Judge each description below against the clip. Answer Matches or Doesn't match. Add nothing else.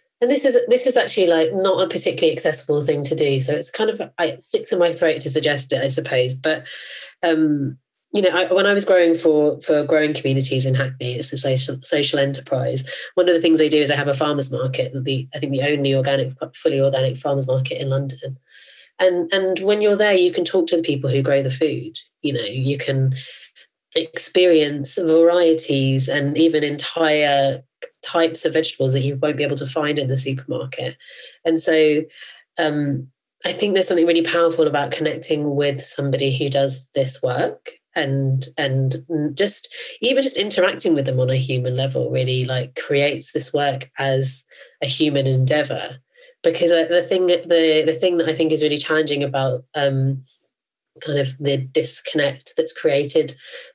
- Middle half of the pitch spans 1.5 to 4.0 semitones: Matches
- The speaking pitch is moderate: Matches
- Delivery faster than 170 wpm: Matches